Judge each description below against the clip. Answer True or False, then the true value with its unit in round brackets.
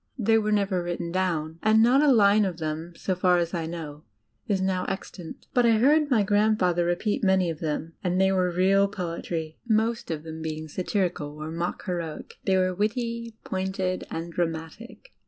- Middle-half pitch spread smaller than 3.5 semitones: False (4.0 semitones)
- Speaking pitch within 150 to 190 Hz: True (185 Hz)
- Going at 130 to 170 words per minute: False (190 wpm)